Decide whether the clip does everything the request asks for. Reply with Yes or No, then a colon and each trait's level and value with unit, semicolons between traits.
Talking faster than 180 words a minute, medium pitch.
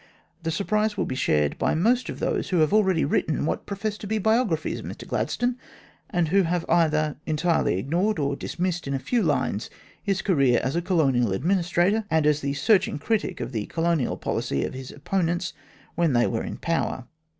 Yes: average, 195 wpm; medium, 165 Hz